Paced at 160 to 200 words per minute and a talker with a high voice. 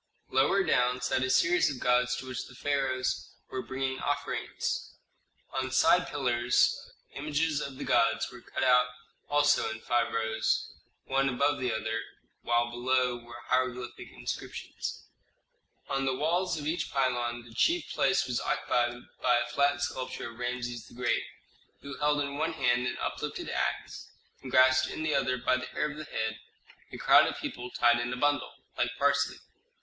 No: average, 170 wpm; low, 130 Hz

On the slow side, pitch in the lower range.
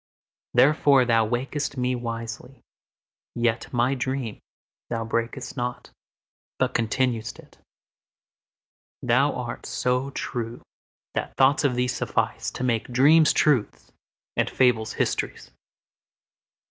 Yes: slow, 95 wpm; low, 125 Hz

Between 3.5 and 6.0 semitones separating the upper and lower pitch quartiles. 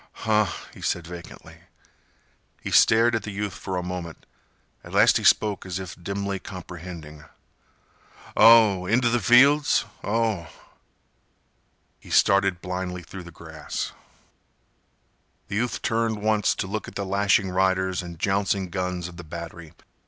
No: average, 3.1 semitones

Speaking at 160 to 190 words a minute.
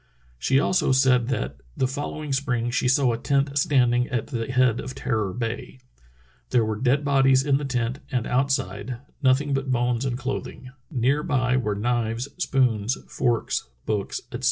Yes: average, 170 wpm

